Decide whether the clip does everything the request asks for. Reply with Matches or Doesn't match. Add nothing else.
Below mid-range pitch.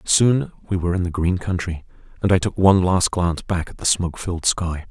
Matches